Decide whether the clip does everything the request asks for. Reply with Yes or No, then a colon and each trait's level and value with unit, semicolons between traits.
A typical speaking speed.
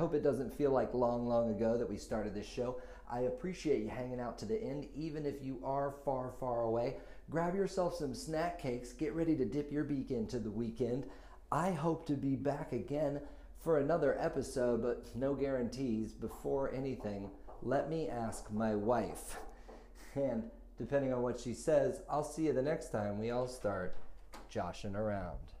Yes: average, 185 wpm